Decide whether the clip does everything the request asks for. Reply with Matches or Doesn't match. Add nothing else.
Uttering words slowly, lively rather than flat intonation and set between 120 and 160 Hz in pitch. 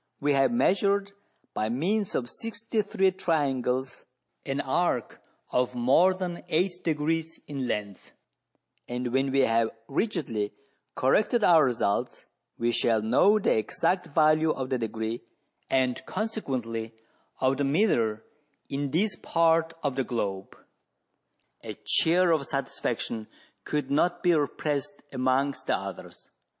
Matches